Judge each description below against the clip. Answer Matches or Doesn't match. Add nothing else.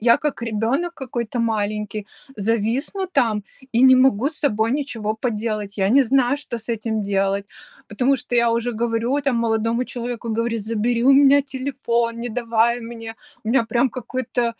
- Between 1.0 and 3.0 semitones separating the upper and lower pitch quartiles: Matches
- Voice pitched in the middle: Doesn't match